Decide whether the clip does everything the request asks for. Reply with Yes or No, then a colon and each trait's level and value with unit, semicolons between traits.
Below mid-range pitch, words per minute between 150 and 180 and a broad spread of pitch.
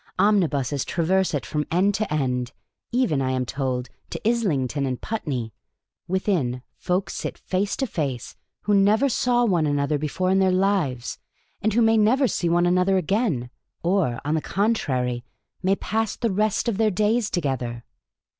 No: medium, 180 Hz; average, 165 wpm; wide, 7.2 semitones